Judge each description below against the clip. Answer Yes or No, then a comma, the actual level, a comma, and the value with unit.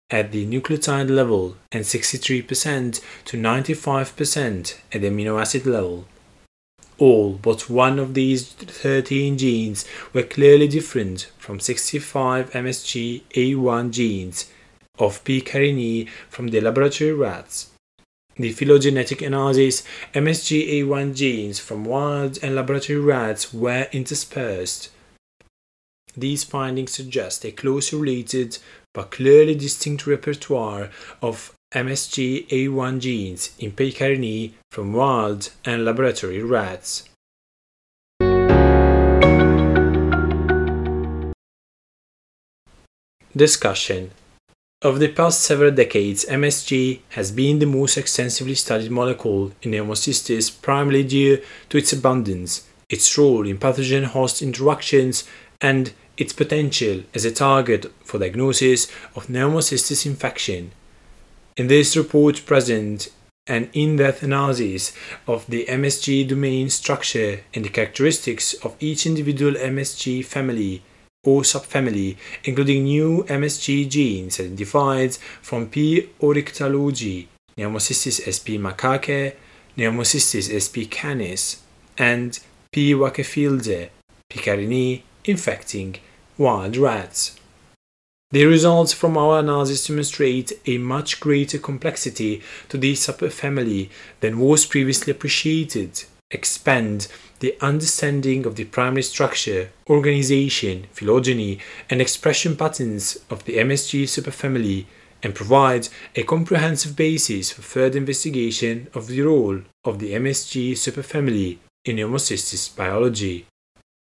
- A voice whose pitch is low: Yes, low, 130 Hz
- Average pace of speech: No, slow, 105 wpm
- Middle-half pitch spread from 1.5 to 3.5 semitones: No, average, 4.6 semitones